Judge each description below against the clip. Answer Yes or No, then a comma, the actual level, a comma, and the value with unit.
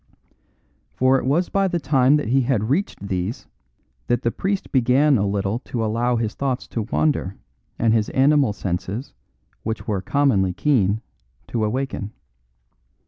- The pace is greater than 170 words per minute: No, average, 150 wpm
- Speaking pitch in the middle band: No, low, 120 Hz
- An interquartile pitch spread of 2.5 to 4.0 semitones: No, average, 4.6 semitones